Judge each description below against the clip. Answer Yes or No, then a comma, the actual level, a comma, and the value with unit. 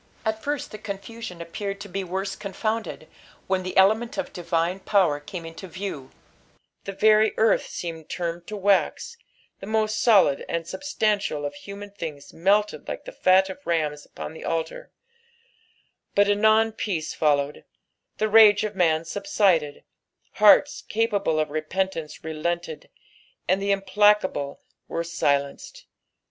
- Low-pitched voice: No, high, 195 Hz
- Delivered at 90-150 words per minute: Yes, average, 140 wpm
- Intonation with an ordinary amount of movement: Yes, average, 4.4 semitones